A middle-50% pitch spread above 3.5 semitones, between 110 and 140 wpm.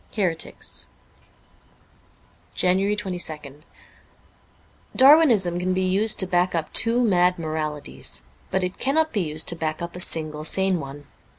Yes: average, 3.9 semitones; slow, 135 wpm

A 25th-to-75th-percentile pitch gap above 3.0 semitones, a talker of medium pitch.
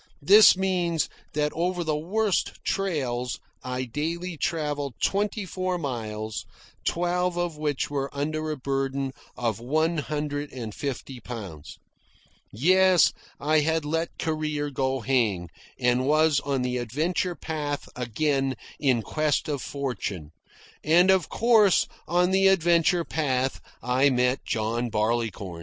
Yes: average, 5.0 semitones; medium, 145 Hz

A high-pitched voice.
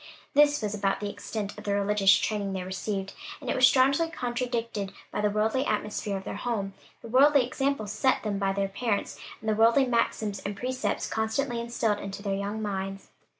Yes: high, 215 Hz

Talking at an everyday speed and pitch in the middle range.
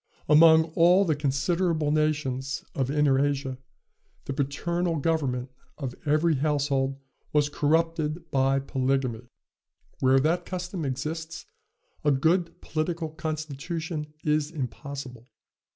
No: slow, 105 wpm; medium, 150 Hz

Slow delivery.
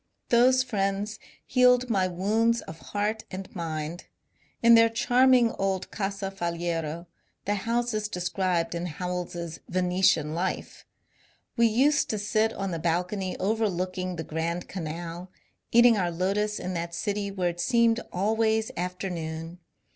No: average, 145 wpm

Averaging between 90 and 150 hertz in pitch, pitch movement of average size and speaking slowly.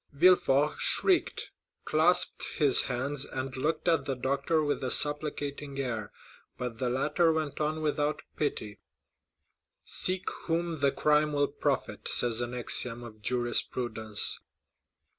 Yes: medium, 140 Hz; average, 3.6 semitones; slow, 130 wpm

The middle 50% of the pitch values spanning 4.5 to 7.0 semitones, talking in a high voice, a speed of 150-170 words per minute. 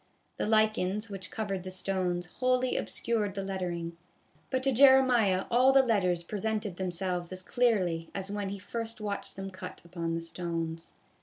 No: average, 3.9 semitones; high, 195 Hz; average, 160 wpm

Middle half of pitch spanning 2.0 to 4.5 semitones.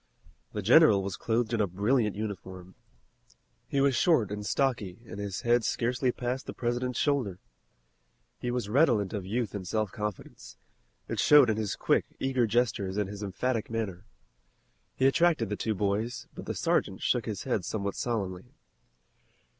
Yes: average, 3.6 semitones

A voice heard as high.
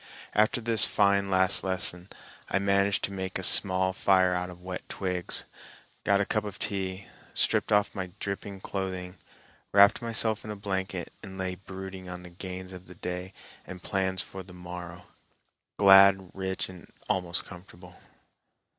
No: very low, 95 Hz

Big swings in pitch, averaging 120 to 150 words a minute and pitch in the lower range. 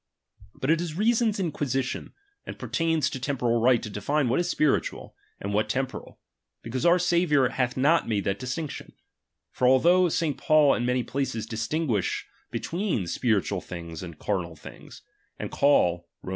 No: wide, 6.8 semitones; average, 165 wpm; low, 130 Hz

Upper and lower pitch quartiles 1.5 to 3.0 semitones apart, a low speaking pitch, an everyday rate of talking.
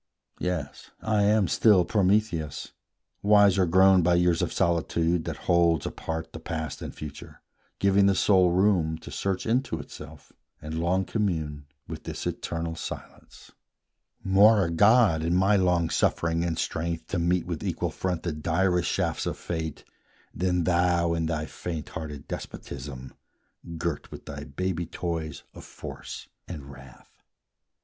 Yes: average, 2.7 semitones; very low, 85 Hz; average, 145 wpm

